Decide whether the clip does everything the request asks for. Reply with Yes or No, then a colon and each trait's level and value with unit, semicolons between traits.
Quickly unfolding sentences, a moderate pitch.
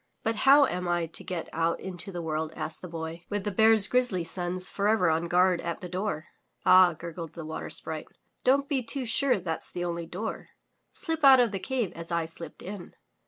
Yes: fast, 210 wpm; medium, 180 Hz